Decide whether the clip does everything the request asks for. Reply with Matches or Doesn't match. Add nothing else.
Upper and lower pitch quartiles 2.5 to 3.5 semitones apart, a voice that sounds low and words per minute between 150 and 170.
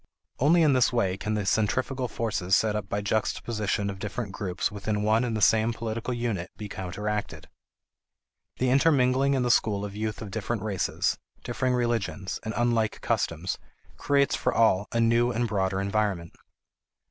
Matches